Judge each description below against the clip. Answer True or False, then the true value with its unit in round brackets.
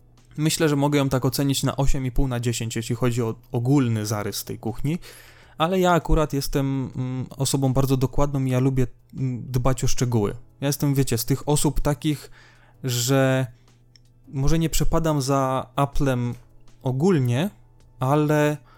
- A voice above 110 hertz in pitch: True (130 Hz)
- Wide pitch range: False (2.9 semitones)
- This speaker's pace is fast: False (145 wpm)